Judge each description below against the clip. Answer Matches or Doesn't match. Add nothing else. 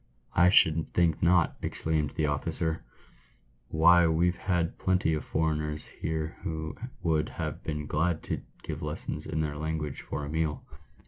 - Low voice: Matches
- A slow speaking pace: Doesn't match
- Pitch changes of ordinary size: Doesn't match